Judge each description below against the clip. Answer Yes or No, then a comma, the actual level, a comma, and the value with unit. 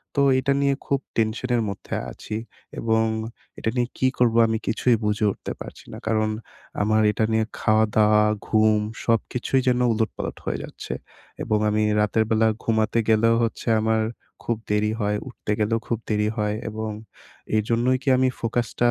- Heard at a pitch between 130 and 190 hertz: No, low, 110 Hz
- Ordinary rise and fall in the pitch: No, narrow, 1.6 semitones